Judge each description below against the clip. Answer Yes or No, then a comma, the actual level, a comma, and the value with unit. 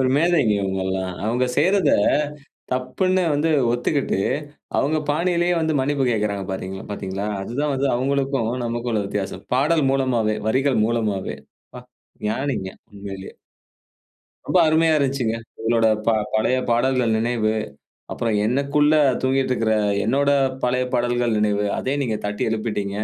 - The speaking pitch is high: No, low, 120 Hz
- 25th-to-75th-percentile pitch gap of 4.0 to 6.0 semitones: Yes, average, 4.6 semitones